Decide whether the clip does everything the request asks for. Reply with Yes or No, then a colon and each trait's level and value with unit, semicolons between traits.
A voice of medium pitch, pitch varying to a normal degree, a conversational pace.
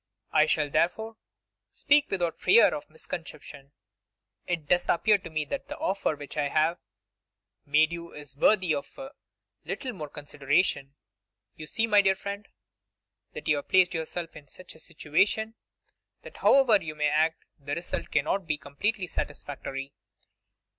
Yes: medium, 165 Hz; average, 4.8 semitones; average, 155 wpm